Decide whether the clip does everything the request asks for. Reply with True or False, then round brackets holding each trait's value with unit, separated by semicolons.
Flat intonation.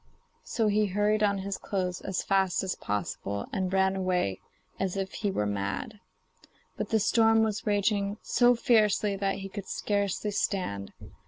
True (2.1 semitones)